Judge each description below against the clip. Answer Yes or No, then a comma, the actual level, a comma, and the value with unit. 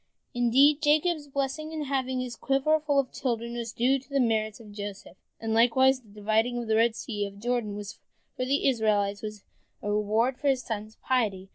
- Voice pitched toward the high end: Yes, high, 240 Hz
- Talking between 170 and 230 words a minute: Yes, fast, 205 wpm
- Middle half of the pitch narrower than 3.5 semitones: No, average, 3.9 semitones